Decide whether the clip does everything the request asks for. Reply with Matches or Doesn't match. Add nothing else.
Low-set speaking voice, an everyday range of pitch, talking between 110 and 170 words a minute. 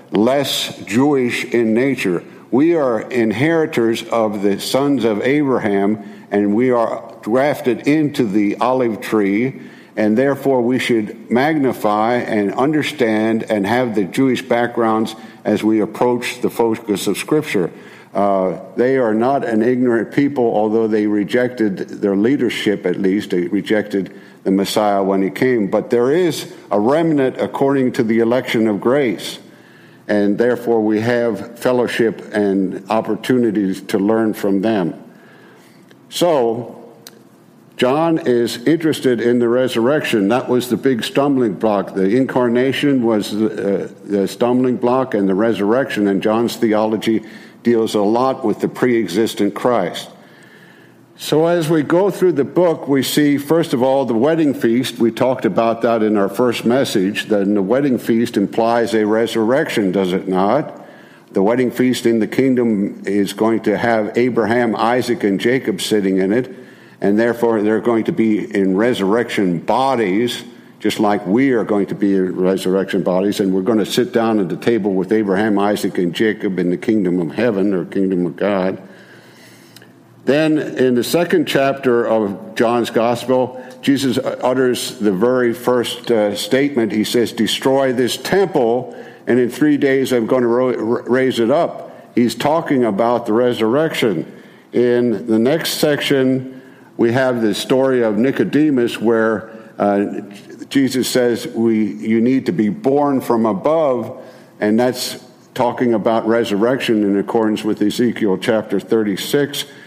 Matches